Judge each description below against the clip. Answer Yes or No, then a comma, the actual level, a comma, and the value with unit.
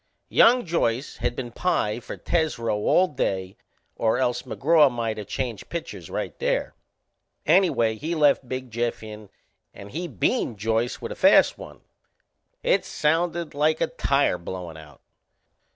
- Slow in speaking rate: No, average, 150 wpm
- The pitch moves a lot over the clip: Yes, wide, 6.3 semitones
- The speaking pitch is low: Yes, low, 120 Hz